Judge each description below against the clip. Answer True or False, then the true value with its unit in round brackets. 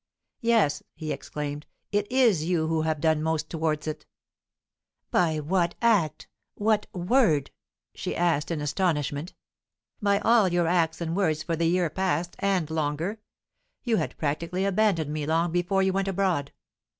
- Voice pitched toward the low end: False (170 Hz)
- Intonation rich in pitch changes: False (3.8 semitones)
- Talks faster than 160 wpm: False (150 wpm)